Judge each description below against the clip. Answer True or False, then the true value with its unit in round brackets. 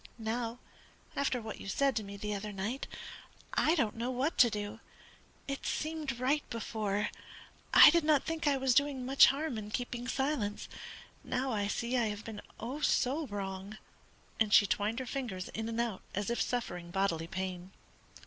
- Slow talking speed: False (175 wpm)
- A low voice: False (235 Hz)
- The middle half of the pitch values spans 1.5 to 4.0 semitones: False (4.5 semitones)